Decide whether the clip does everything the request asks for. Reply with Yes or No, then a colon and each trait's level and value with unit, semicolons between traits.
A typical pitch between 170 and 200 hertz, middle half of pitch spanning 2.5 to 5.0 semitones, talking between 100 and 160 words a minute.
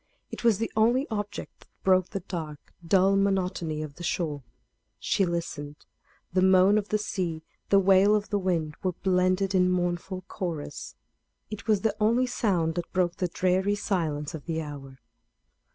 No: medium, 185 Hz; average, 3.3 semitones; average, 170 wpm